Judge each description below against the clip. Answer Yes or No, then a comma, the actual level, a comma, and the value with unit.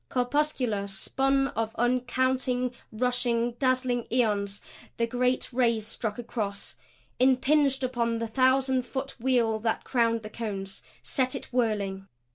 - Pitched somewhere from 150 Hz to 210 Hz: No, high, 245 Hz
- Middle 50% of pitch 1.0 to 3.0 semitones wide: Yes, narrow, 2.5 semitones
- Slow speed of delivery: Yes, slow, 120 wpm